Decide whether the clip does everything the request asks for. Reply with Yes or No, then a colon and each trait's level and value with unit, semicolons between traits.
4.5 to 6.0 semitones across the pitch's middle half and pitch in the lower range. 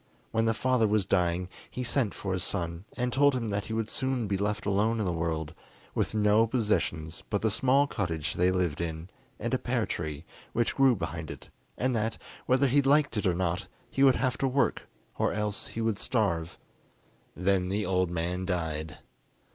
Yes: average, 5.3 semitones; low, 100 Hz